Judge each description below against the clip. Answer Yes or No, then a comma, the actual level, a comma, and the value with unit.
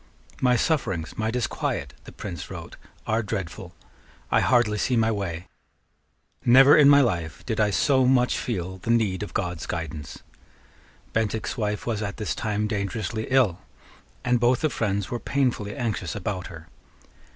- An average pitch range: Yes, average, 4.4 semitones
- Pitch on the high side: No, low, 110 Hz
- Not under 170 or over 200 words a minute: No, average, 155 wpm